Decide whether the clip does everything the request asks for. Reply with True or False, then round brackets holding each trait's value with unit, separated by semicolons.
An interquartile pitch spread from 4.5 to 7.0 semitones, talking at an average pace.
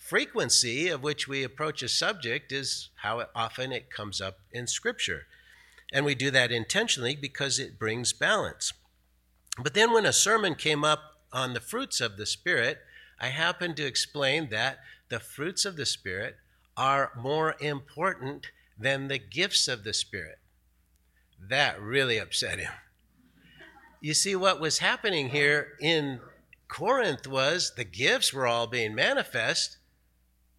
True (5.1 semitones; 145 wpm)